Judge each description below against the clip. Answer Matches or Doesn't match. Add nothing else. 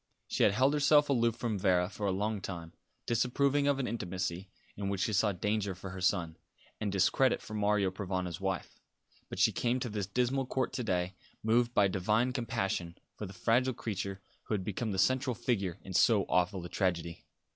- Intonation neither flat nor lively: Matches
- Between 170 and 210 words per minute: Matches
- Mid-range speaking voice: Doesn't match